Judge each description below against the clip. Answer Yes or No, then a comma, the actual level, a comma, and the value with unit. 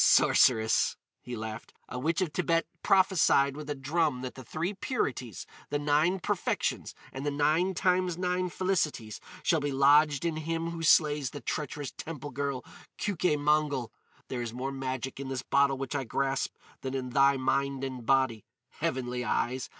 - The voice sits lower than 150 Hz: Yes, medium, 140 Hz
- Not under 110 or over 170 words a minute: Yes, average, 165 wpm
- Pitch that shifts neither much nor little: Yes, average, 3.7 semitones